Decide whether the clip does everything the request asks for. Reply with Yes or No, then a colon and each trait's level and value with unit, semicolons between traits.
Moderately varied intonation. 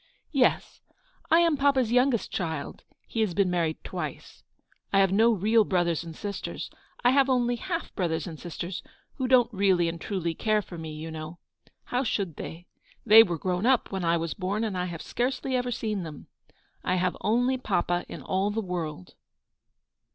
No: wide, 5.8 semitones